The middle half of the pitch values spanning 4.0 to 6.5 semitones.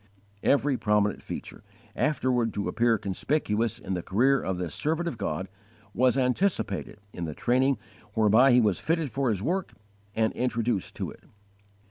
Yes: average, 4.9 semitones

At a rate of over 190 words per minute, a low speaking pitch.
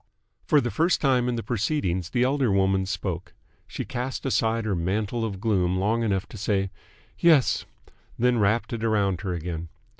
No: average, 175 wpm; low, 110 Hz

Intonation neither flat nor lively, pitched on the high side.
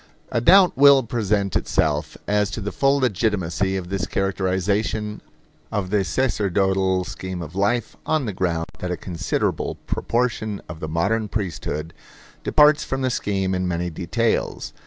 No: average, 3.7 semitones; low, 100 Hz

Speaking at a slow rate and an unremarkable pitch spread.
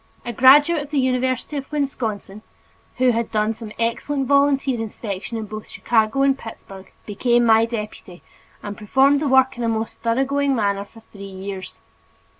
No: average, 165 wpm; average, 4.0 semitones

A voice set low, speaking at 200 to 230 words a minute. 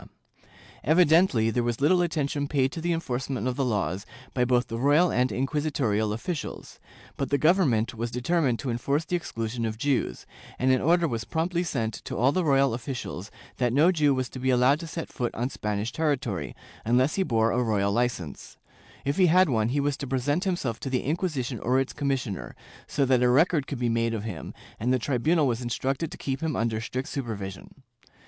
Yes: low, 130 Hz; fast, 205 wpm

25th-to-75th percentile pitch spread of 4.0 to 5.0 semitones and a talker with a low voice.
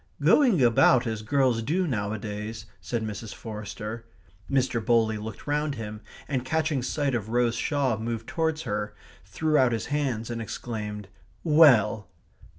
Yes: average, 4.4 semitones; low, 115 Hz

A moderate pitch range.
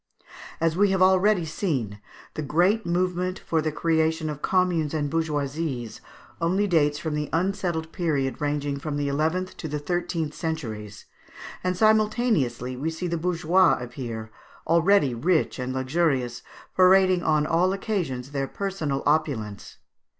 Yes: average, 4.4 semitones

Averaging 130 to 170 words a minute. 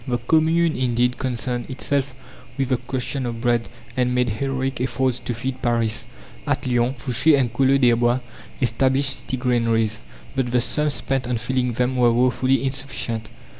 Yes: average, 160 wpm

